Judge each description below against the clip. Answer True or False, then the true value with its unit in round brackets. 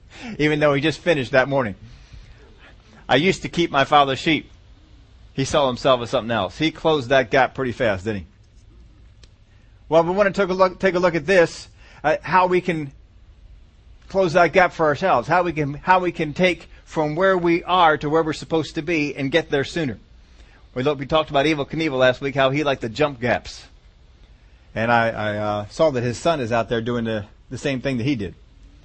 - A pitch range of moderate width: False (6.5 semitones)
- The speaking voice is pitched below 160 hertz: True (140 Hz)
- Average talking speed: False (215 wpm)